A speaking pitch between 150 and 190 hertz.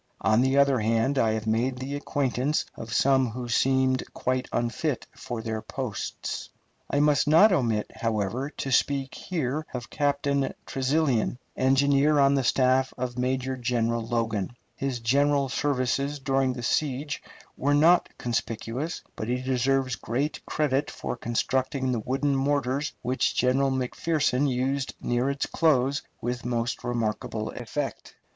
No: low, 130 Hz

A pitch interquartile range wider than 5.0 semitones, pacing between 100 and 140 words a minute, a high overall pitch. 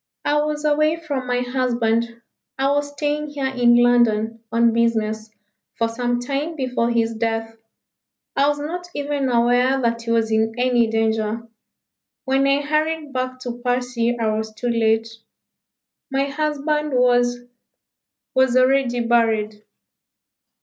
No: average, 3.3 semitones; slow, 135 wpm; high, 245 Hz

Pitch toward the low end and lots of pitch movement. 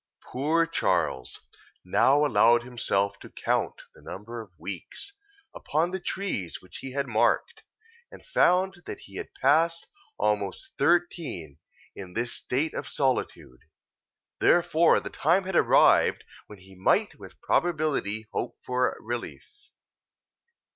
Yes: low, 130 Hz; wide, 8.3 semitones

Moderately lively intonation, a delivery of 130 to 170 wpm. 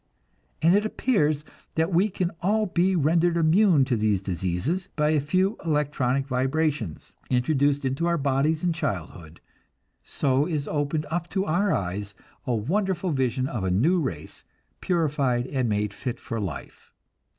No: wide, 5.7 semitones; average, 150 wpm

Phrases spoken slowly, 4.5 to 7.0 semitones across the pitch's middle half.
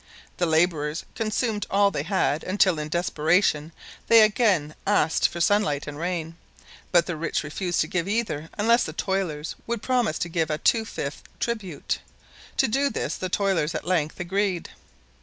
No: average, 165 wpm; average, 4.8 semitones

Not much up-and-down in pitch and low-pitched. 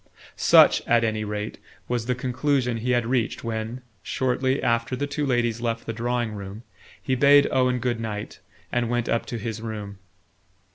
Yes: narrow, 2.1 semitones; low, 120 Hz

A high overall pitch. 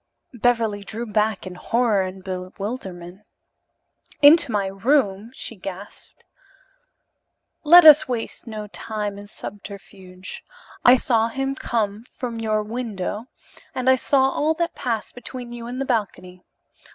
Yes: high, 220 Hz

